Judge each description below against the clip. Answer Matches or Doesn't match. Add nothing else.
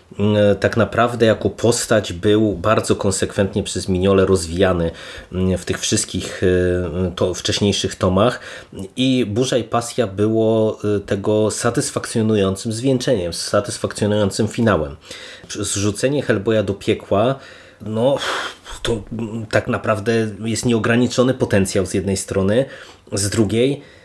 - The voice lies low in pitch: Matches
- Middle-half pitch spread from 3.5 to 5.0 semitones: Doesn't match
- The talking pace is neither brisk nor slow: Doesn't match